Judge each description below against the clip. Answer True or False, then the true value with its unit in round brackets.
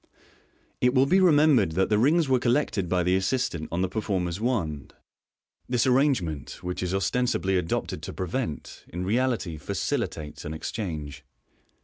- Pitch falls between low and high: False (95 Hz)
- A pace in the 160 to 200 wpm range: False (150 wpm)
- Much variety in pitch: True (6.8 semitones)